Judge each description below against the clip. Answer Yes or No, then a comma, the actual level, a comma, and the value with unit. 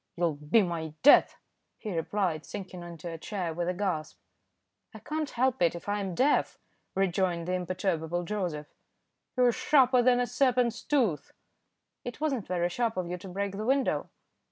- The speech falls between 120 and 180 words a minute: Yes, average, 170 wpm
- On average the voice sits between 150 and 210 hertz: Yes, high, 190 Hz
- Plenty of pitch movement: Yes, wide, 5.9 semitones